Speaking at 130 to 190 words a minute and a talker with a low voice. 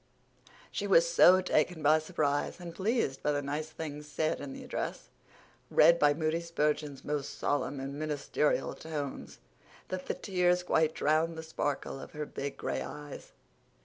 No: average, 160 wpm; medium, 155 Hz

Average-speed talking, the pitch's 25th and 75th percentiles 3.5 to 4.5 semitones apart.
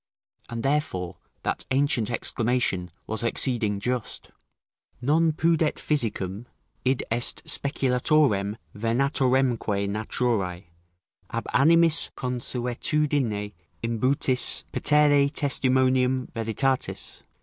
No: slow, 80 wpm; average, 3.9 semitones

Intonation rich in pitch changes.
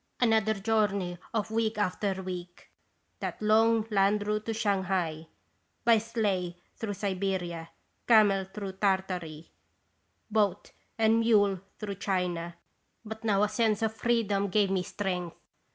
No: average, 2.7 semitones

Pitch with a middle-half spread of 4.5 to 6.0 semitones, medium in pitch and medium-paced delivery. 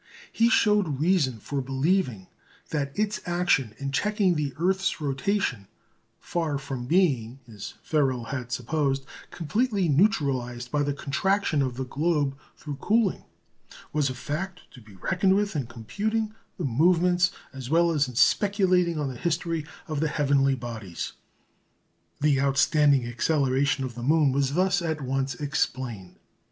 Yes: average, 5.2 semitones; medium, 145 Hz; average, 145 wpm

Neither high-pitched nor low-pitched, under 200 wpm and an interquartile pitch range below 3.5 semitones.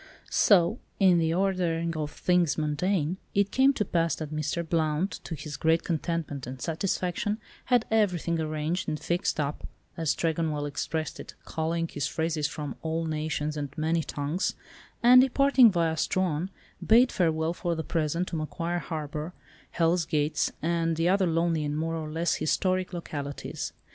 Yes: medium, 165 Hz; average, 160 wpm; narrow, 2.6 semitones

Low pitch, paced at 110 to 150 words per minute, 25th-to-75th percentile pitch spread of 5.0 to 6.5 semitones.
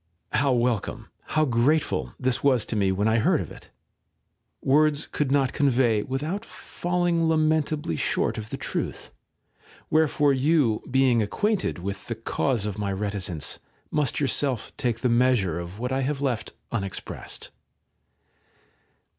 Yes: low, 130 Hz; average, 140 wpm; wide, 5.4 semitones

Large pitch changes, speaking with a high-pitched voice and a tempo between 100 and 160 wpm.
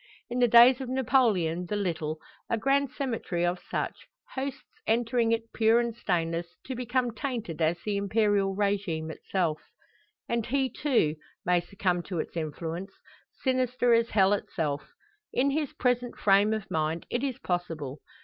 Yes: wide, 6.0 semitones; high, 210 Hz; average, 155 wpm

